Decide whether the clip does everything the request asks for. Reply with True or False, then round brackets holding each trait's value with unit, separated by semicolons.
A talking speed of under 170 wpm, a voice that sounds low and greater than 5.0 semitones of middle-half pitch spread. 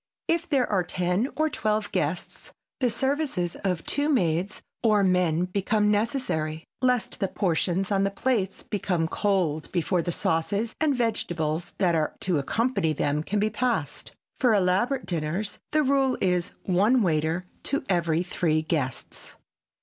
False (150 wpm; 190 Hz; 5.5 semitones)